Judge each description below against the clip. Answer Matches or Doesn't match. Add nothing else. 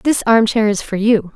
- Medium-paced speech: Doesn't match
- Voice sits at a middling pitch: Doesn't match